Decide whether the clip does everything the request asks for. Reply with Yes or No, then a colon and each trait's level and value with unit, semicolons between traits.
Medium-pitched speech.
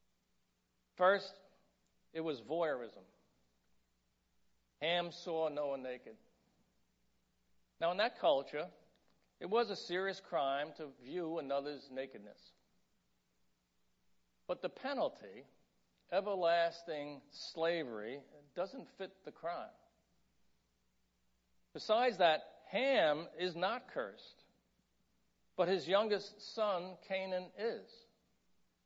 Yes: medium, 150 Hz